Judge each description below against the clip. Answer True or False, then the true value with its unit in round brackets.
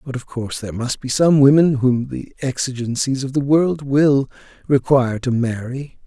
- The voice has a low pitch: True (130 Hz)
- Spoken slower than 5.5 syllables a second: True (5.0 syllables/s)